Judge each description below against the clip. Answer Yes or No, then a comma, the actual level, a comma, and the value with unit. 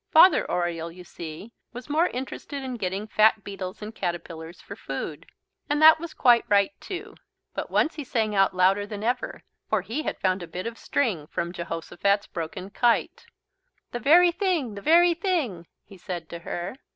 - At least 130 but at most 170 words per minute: No, average, 180 wpm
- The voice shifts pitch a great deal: Yes, wide, 7.5 semitones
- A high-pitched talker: Yes, high, 210 Hz